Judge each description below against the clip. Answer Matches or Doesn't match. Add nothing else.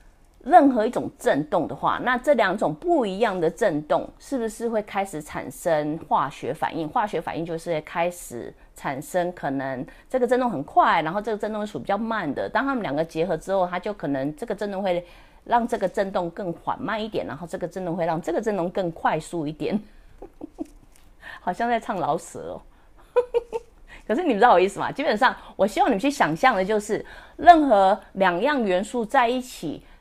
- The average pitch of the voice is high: Matches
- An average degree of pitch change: Doesn't match